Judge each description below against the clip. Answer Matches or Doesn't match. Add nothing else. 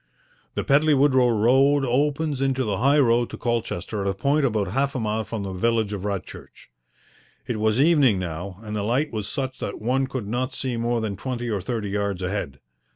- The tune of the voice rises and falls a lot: Doesn't match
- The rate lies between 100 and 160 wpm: Doesn't match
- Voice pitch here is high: Doesn't match